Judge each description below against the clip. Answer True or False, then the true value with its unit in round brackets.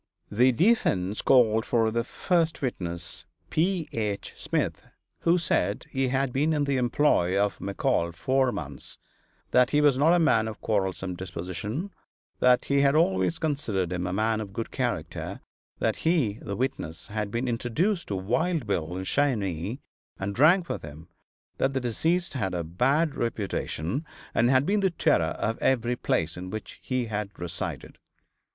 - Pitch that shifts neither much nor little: False (6.8 semitones)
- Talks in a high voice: False (115 Hz)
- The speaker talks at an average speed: True (165 wpm)